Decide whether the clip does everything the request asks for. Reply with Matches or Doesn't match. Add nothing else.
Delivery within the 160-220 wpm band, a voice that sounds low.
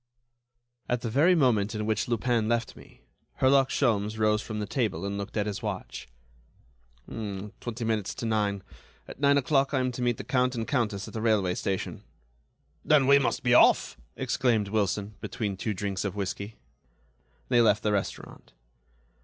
Matches